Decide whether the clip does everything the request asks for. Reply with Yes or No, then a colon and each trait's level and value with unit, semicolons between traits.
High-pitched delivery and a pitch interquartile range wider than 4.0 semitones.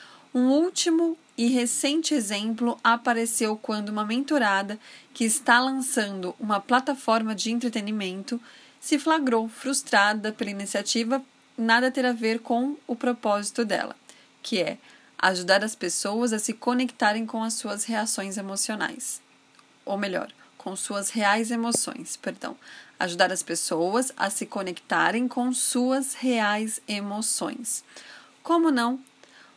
No: high, 230 Hz; average, 3.6 semitones